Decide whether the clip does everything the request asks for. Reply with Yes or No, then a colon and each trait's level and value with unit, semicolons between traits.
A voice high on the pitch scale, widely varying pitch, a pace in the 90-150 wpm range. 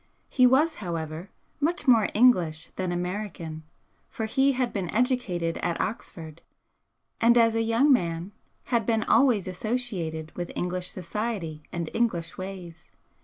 Yes: high, 195 Hz; wide, 5.8 semitones; slow, 135 wpm